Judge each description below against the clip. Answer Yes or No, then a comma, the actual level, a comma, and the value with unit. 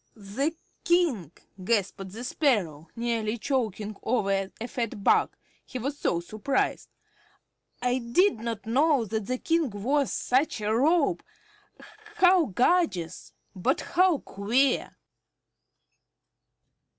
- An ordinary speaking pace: No, slow, 110 wpm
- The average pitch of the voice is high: Yes, high, 235 Hz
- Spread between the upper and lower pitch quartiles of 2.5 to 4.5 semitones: No, wide, 5.5 semitones